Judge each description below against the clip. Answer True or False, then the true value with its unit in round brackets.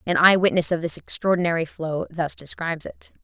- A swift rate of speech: False (185 wpm)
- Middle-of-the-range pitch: True (165 Hz)